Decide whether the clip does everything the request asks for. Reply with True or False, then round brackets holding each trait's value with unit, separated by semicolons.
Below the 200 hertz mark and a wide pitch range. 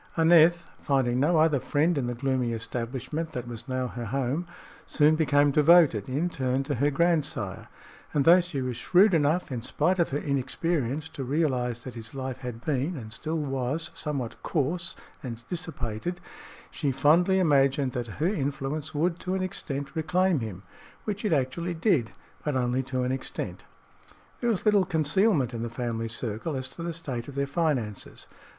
False (140 Hz; 4.6 semitones)